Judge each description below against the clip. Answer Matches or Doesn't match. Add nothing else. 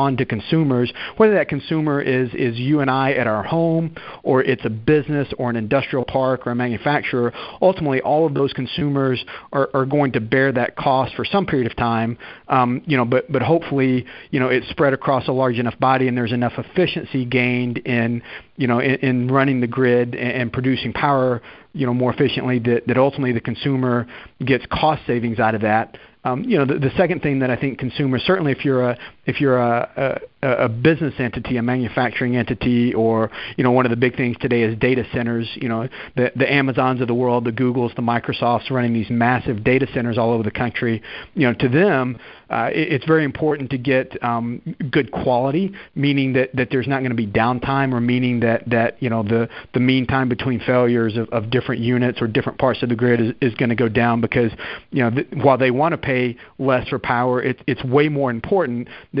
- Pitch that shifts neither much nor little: Doesn't match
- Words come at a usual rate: Doesn't match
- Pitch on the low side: Matches